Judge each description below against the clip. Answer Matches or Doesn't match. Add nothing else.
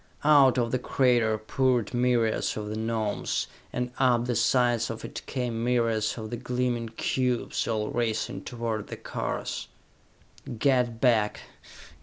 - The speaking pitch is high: Doesn't match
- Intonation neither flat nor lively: Doesn't match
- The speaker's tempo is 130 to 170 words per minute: Matches